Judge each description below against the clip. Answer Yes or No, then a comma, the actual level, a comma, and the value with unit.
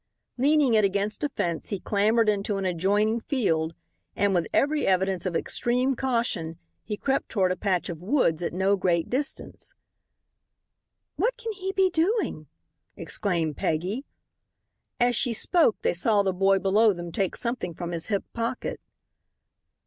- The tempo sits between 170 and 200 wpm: No, average, 155 wpm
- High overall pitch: Yes, high, 205 Hz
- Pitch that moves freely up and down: Yes, wide, 5.7 semitones